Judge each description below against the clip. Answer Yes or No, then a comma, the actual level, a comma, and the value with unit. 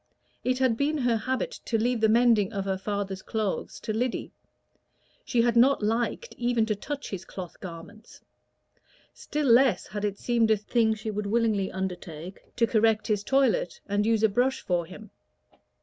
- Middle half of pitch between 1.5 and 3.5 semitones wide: Yes, average, 3.2 semitones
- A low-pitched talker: No, high, 220 Hz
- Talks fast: No, average, 175 wpm